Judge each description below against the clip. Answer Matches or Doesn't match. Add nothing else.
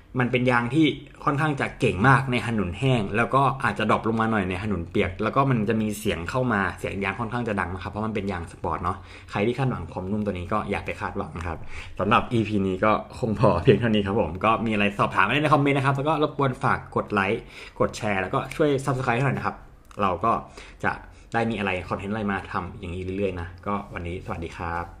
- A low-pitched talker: Matches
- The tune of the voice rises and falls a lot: Doesn't match